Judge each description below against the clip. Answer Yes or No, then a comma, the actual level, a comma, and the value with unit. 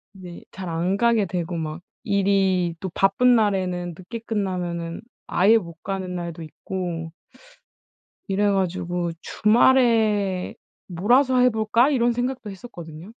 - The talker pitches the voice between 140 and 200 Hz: Yes, high, 190 Hz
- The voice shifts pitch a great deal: No, average, 4.1 semitones